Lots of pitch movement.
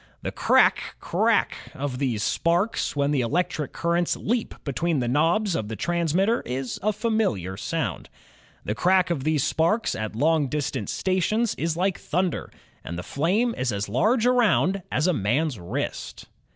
Yes: wide, 6.6 semitones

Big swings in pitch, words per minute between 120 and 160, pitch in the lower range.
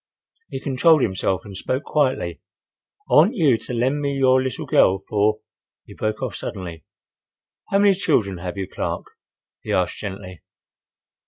Yes: wide, 6.9 semitones; average, 155 wpm; low, 120 Hz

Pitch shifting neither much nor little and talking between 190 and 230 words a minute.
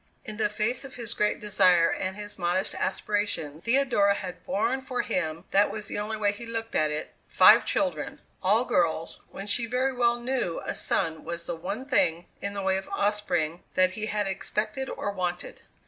Yes: average, 3.9 semitones; average, 195 wpm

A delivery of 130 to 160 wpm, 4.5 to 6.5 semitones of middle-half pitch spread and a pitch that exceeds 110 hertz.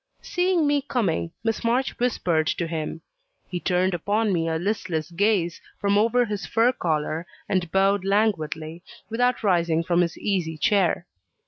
Yes: average, 150 wpm; average, 4.9 semitones; high, 190 Hz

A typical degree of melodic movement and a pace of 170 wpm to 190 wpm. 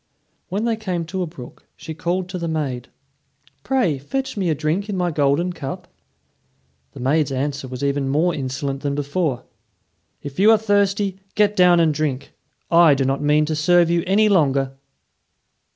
Yes: average, 4.9 semitones; average, 175 wpm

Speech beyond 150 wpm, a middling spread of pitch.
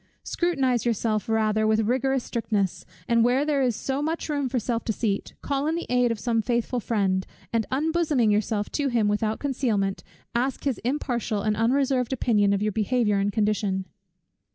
Yes: average, 175 wpm; average, 3.8 semitones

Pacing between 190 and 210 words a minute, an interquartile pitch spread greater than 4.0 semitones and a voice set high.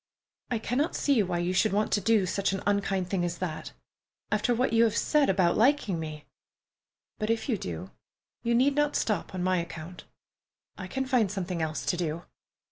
Yes: average, 195 wpm; average, 4.7 semitones; high, 195 Hz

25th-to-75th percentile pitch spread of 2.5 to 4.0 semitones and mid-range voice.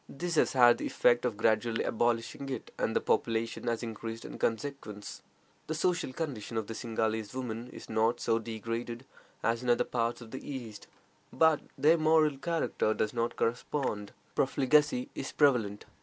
No: average, 3.4 semitones; low, 120 Hz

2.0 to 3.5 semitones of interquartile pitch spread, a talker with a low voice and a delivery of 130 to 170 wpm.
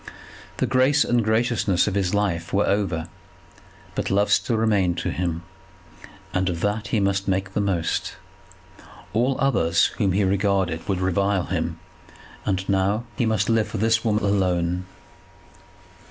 Yes: average, 2.8 semitones; low, 100 Hz; average, 150 wpm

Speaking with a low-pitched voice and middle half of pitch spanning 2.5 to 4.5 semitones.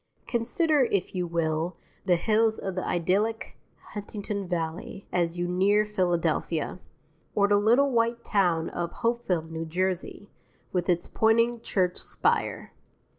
No: high, 190 Hz; average, 4.2 semitones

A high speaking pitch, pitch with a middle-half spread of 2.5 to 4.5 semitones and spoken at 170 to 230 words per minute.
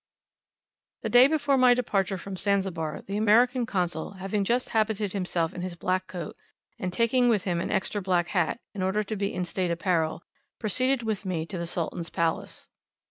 Yes: high, 195 Hz; average, 3.7 semitones; average, 185 wpm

